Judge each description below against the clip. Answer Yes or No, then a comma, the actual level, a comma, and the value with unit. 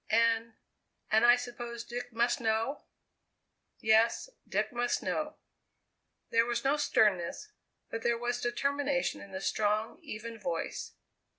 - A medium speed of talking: No, slow, 125 wpm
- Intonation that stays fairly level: Yes, narrow, 1.8 semitones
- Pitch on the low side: No, high, 235 Hz